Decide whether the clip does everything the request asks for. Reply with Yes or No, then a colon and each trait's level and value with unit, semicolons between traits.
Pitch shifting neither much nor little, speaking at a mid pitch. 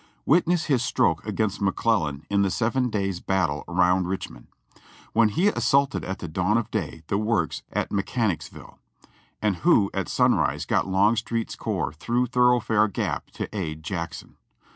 No: average, 4.3 semitones; low, 100 Hz